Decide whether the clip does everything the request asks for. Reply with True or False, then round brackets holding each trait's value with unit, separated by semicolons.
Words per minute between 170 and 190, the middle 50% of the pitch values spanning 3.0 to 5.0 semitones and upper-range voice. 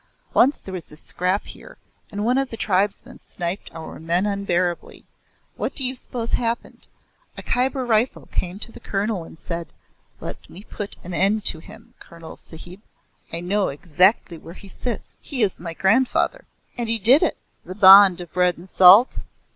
True (180 wpm; 4.4 semitones; 195 Hz)